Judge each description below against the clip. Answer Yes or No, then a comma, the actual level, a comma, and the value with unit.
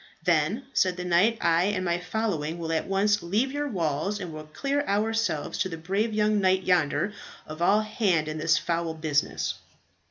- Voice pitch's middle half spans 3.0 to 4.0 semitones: No, average, 4.4 semitones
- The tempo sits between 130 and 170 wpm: No, average, 185 wpm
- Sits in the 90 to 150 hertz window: No, medium, 180 Hz